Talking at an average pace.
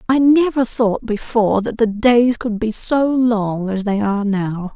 Yes: average, 190 wpm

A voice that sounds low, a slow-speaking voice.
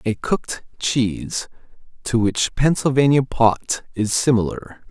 Yes: low, 120 Hz; slow, 110 wpm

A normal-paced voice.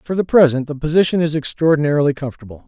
Yes: average, 180 wpm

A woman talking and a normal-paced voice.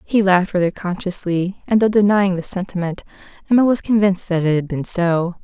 Yes: female; average, 190 wpm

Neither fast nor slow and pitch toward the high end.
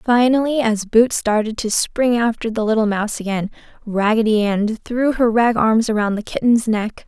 Yes: average, 180 wpm; high, 225 Hz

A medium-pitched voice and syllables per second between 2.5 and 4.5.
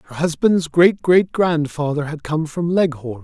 Yes: medium, 160 Hz; 4.3 syllables/s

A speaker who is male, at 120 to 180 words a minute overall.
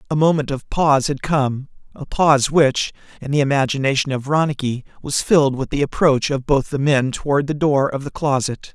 No: male; average, 200 wpm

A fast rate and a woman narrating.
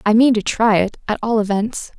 Yes: fast, 240 wpm; female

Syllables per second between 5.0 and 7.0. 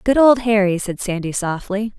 No: 4.8 syllables/s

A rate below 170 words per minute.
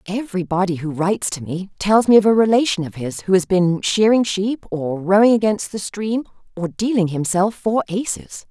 No: average, 190 wpm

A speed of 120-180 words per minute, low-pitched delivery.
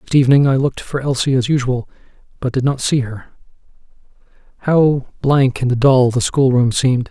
Yes: average, 175 wpm; low, 130 Hz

